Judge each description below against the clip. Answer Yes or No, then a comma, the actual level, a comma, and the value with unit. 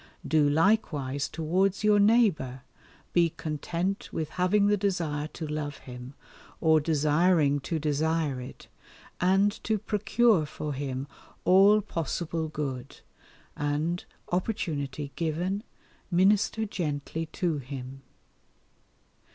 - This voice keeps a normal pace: No, slow, 105 wpm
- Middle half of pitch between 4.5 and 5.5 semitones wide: Yes, average, 4.8 semitones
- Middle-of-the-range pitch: Yes, medium, 160 Hz